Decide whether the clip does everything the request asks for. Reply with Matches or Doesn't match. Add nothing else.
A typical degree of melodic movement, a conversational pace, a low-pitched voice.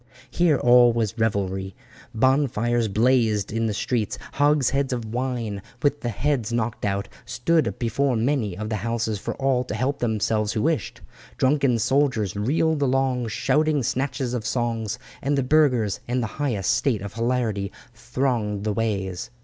Matches